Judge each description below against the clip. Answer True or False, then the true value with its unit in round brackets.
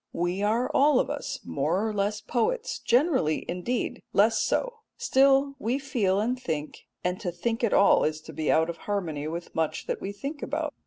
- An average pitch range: False (7.4 semitones)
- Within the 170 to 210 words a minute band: True (195 wpm)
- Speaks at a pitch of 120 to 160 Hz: False (215 Hz)